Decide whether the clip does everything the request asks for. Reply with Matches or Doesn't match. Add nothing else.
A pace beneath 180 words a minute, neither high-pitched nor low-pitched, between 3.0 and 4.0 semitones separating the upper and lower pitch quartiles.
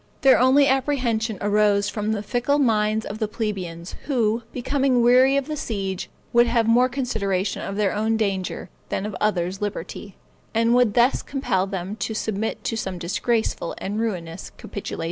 Doesn't match